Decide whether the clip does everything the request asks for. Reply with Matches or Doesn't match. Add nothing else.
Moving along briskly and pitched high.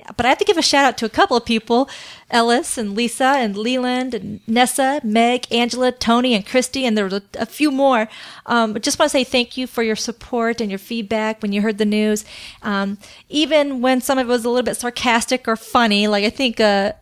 Matches